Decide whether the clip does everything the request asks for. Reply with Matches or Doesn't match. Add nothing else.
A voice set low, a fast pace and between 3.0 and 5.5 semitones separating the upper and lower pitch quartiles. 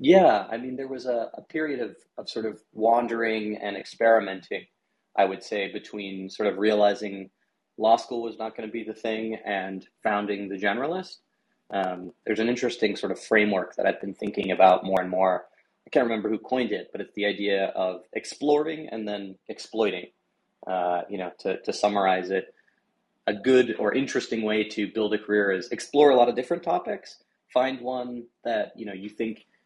Doesn't match